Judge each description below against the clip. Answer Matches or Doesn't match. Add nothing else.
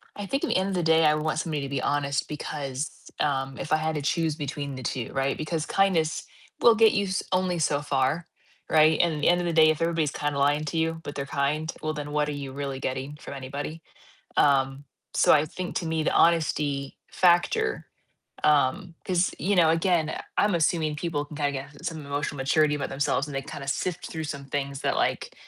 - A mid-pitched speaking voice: Matches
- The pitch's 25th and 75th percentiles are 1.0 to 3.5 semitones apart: Matches